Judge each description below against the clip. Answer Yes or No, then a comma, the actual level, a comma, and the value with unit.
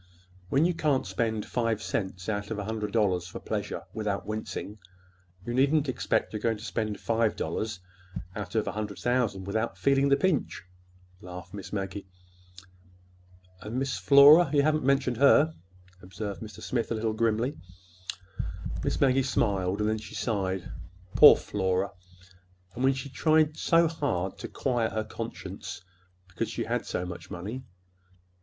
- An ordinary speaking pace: Yes, average, 150 wpm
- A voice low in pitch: Yes, low, 110 Hz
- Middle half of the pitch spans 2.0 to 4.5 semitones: No, average, 5.2 semitones